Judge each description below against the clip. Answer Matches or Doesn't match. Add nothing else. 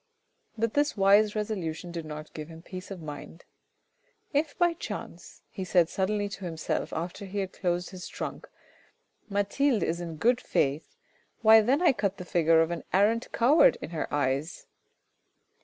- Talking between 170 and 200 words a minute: Matches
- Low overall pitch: Doesn't match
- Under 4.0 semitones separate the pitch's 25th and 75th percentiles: Doesn't match